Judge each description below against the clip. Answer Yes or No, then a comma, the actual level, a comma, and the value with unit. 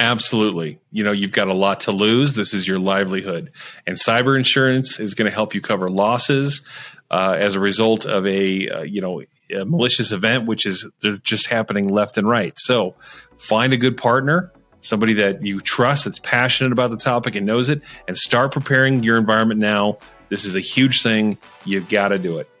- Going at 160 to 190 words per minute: No, average, 200 wpm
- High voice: No, low, 110 Hz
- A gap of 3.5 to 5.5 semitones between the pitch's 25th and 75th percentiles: Yes, average, 3.9 semitones